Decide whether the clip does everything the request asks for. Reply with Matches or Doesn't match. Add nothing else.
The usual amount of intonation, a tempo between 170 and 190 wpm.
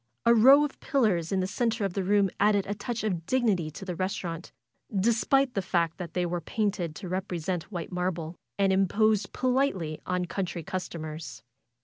Matches